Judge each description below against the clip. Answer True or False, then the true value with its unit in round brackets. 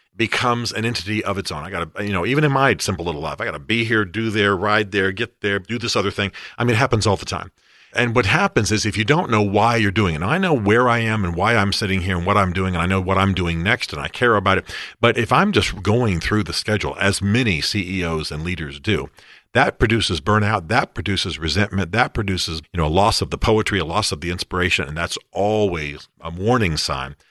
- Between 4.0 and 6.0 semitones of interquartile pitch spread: False (3.5 semitones)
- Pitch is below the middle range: True (100 Hz)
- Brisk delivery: True (260 wpm)